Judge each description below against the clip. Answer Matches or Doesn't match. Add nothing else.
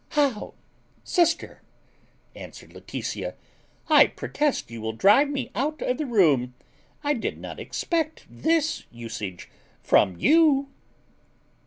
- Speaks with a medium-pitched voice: Doesn't match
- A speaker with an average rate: Doesn't match